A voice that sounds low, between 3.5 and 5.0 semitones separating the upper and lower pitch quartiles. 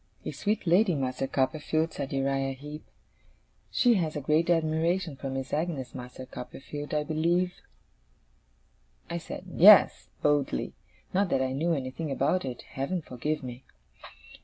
No: medium, 150 Hz; average, 4.0 semitones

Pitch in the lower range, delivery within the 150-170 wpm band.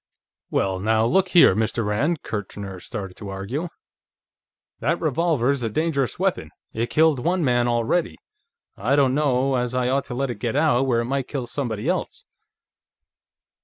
Yes: low, 125 Hz; average, 165 wpm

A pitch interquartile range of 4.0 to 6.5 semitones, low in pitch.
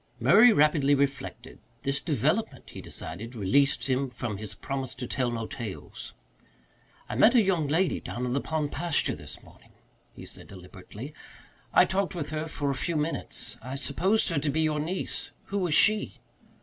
No: average, 4.4 semitones; medium, 145 Hz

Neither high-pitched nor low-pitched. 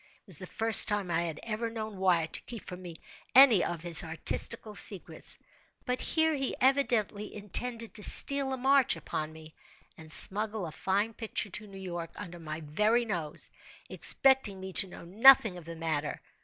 No: high, 205 Hz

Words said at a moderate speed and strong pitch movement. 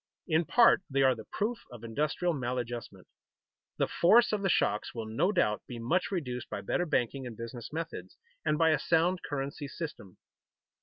Yes: average, 175 wpm; wide, 6.3 semitones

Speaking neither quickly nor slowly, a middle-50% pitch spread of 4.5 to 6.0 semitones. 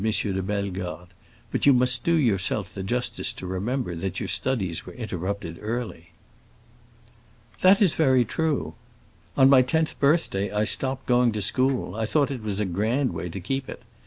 Yes: average, 170 wpm; wide, 5.5 semitones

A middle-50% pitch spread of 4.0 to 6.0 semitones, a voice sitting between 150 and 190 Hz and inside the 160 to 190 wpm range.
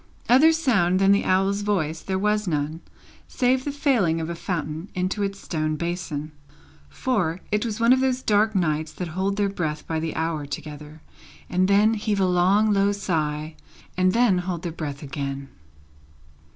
Yes: average, 4.7 semitones; medium, 185 Hz; average, 170 wpm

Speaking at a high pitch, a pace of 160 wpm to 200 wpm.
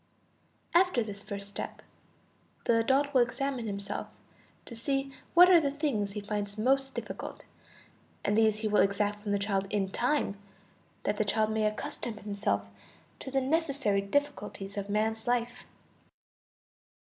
No: high, 220 Hz; average, 145 wpm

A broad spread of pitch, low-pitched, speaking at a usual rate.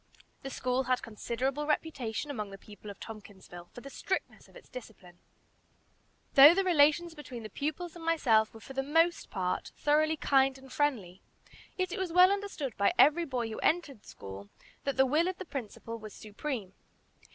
No: wide, 6.3 semitones; very high, 270 Hz; average, 180 wpm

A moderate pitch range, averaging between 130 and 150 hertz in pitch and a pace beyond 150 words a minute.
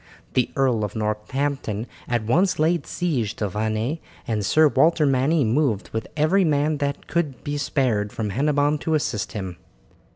No: wide, 5.7 semitones; low, 135 Hz; average, 160 wpm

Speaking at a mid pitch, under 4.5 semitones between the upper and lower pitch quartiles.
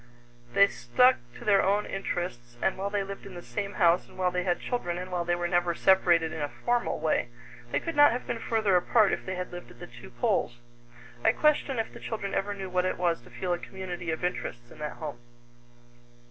Yes: medium, 180 Hz; narrow, 2.6 semitones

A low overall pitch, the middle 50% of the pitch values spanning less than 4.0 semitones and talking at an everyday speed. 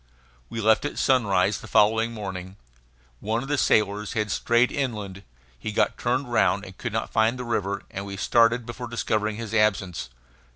Yes: low, 110 Hz; average, 2.8 semitones; average, 175 wpm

